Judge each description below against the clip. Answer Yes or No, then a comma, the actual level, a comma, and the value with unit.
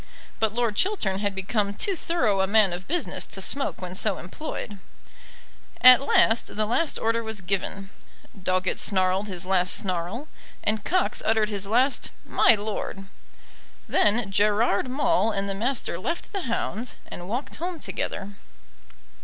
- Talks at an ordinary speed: Yes, average, 150 wpm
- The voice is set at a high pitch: Yes, high, 210 Hz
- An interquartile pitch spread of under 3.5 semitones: No, average, 3.9 semitones